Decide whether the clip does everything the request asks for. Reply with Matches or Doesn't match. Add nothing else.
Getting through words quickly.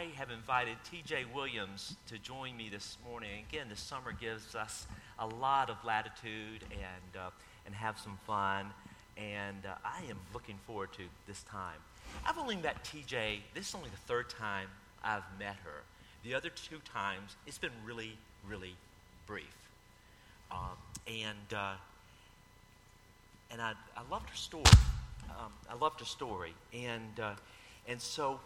Doesn't match